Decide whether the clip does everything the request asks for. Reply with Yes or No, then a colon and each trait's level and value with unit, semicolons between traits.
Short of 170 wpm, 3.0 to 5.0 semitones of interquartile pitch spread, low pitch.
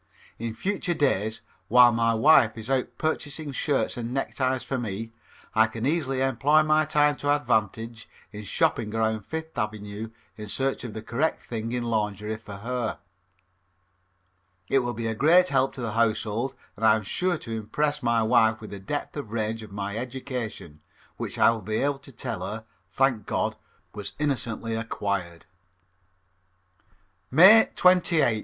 Yes: average, 160 wpm; average, 3.9 semitones; low, 115 Hz